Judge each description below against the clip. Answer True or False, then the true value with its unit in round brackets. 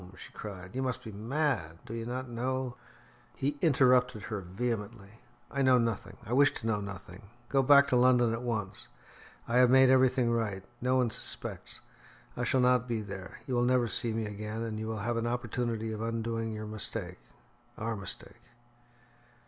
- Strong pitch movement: False (2.8 semitones)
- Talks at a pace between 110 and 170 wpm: False (185 wpm)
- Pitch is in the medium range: False (115 Hz)